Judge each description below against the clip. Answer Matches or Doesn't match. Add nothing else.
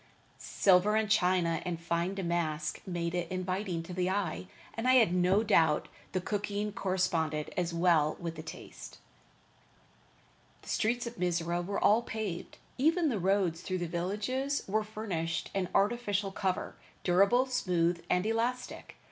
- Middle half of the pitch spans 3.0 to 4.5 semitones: Matches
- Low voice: Doesn't match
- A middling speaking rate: Matches